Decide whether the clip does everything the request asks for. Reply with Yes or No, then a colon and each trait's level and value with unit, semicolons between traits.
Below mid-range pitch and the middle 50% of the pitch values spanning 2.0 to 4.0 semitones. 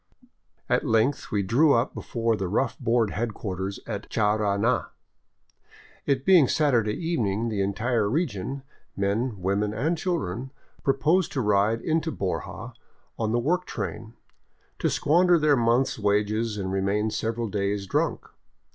No: low, 115 Hz; average, 4.9 semitones